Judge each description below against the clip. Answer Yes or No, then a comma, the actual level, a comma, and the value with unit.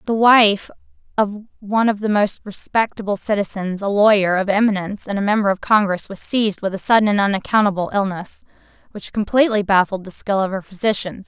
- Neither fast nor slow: Yes, average, 170 wpm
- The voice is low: No, high, 205 Hz